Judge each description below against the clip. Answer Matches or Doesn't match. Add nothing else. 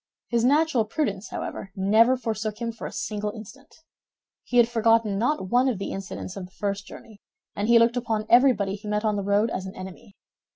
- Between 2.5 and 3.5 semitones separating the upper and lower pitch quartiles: Matches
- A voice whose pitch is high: Matches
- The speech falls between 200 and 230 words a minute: Matches